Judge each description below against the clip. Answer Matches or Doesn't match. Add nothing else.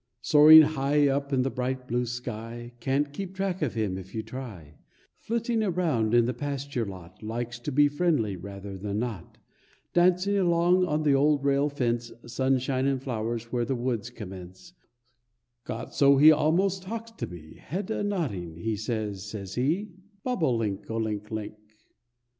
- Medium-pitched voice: Doesn't match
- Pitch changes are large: Matches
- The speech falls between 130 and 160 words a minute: Doesn't match